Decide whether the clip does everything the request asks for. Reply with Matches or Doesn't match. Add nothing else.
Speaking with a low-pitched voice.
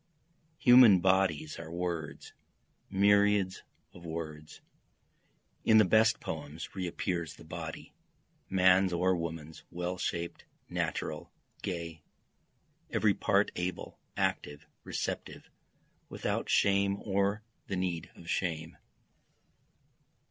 Matches